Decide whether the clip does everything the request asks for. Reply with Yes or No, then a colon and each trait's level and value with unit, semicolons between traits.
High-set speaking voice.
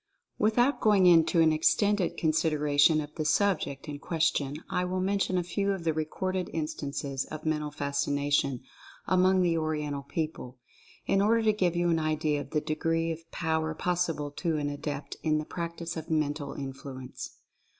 No: medium, 160 Hz